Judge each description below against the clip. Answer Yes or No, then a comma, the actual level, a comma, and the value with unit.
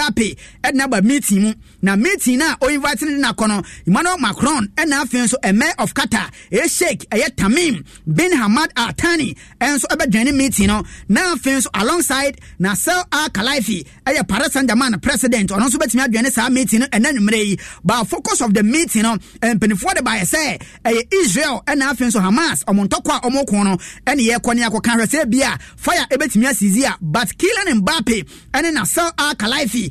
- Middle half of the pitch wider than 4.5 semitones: Yes, average, 5.2 semitones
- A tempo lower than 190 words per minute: No, fast, 205 wpm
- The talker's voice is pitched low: No, high, 245 Hz